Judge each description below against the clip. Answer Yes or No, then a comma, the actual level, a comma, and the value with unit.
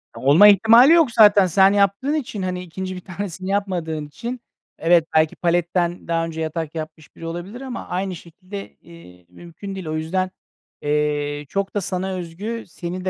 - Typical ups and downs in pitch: Yes, average, 3.3 semitones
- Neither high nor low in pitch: Yes, medium, 180 Hz